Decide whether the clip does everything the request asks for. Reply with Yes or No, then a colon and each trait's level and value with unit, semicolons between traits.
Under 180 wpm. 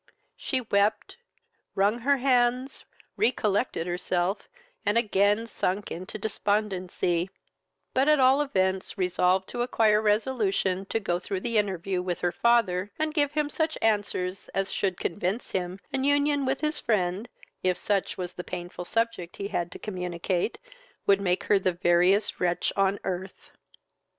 Yes: average, 150 wpm